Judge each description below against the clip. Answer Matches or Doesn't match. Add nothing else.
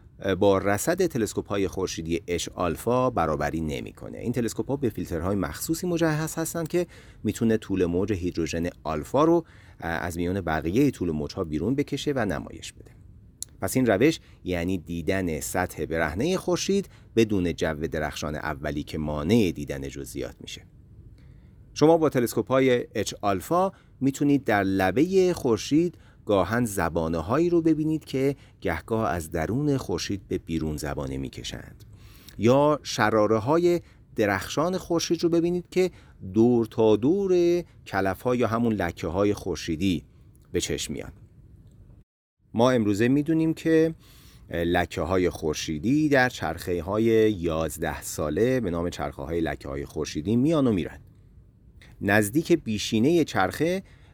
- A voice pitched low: Matches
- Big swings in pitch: Matches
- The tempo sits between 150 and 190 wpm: Doesn't match